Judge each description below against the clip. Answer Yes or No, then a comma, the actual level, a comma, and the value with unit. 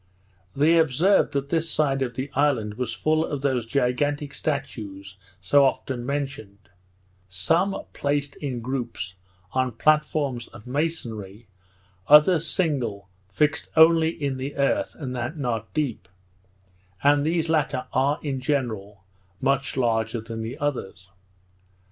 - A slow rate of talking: Yes, slow, 130 wpm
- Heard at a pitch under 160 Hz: Yes, low, 135 Hz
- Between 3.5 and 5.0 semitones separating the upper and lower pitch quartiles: Yes, average, 4.0 semitones